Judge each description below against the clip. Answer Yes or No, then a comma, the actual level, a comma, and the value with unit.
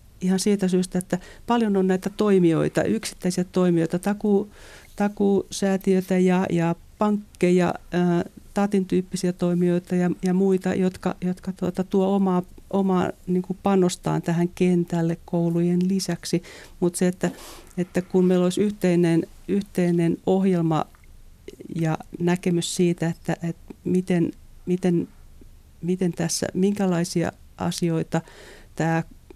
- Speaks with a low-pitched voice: No, medium, 180 Hz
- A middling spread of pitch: No, narrow, 1.6 semitones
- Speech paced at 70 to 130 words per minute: Yes, average, 110 wpm